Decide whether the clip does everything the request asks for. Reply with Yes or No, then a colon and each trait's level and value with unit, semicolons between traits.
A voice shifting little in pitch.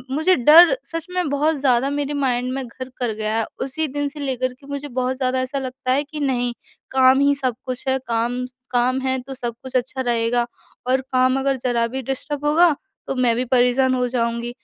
Yes: narrow, 2.2 semitones